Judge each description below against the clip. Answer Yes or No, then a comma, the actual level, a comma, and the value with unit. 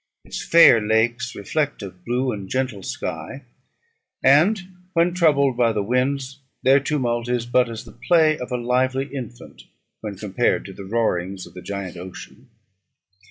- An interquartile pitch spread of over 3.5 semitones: Yes, average, 4.5 semitones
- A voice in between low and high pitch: No, low, 120 Hz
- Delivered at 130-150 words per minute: No, average, 160 wpm